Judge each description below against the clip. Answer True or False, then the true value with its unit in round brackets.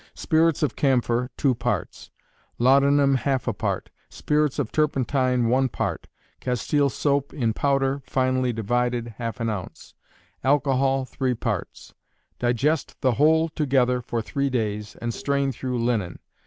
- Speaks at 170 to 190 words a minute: False (135 wpm)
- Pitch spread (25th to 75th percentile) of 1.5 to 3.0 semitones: True (2.6 semitones)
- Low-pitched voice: True (130 Hz)